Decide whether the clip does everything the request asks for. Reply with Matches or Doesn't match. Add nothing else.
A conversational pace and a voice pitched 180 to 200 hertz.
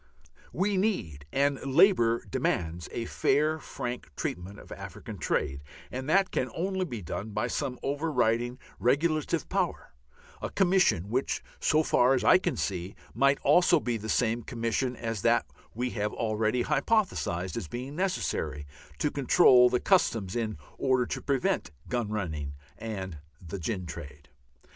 Doesn't match